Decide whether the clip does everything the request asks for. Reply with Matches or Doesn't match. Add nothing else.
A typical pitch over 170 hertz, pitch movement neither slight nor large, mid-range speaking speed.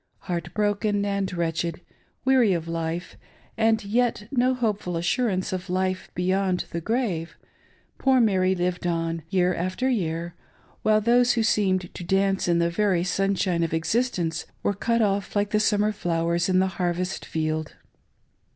Matches